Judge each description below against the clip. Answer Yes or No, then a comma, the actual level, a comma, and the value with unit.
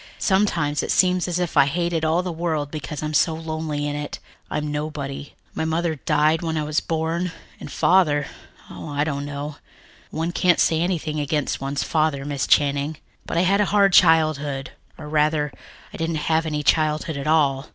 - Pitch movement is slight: Yes, narrow, 2.0 semitones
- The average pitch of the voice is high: No, medium, 155 Hz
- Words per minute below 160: No, average, 185 wpm